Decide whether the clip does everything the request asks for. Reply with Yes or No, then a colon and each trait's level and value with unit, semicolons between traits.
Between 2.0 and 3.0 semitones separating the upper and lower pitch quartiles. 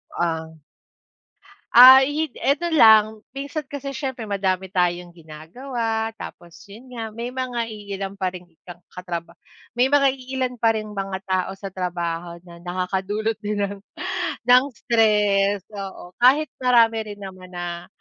No: average, 5.2 semitones